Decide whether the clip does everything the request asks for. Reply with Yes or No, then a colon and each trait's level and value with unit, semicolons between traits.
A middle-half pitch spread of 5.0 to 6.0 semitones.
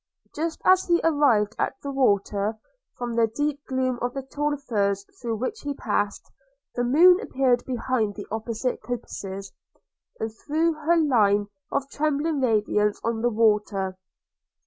Yes: average, 5.3 semitones